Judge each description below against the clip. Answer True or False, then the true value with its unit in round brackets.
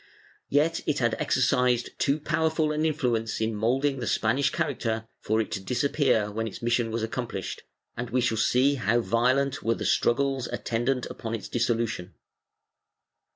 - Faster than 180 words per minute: False (155 wpm)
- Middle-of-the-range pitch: False (120 Hz)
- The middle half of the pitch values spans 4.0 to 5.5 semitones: False (3.5 semitones)